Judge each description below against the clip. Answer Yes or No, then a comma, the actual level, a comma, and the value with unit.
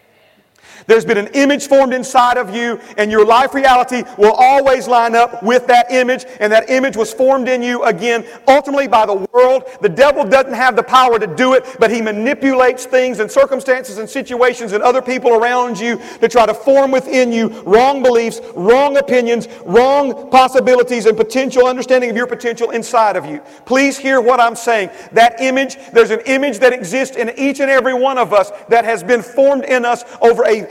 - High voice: Yes, high, 245 Hz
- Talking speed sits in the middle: Yes, average, 195 wpm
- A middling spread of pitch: No, narrow, 2.1 semitones